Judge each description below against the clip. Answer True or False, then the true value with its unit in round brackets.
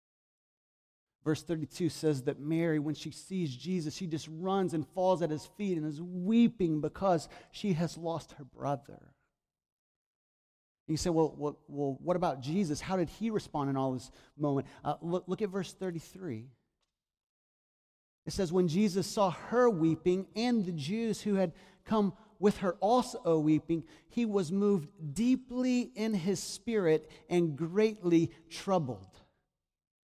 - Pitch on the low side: False (170 Hz)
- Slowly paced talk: False (150 wpm)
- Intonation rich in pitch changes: False (4.2 semitones)